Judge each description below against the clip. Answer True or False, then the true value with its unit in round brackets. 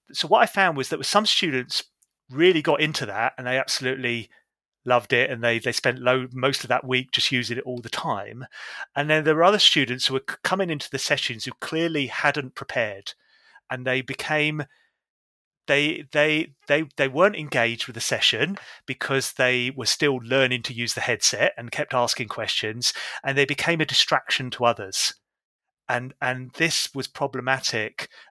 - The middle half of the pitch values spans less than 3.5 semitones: True (2.8 semitones)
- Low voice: True (130 Hz)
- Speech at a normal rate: True (180 wpm)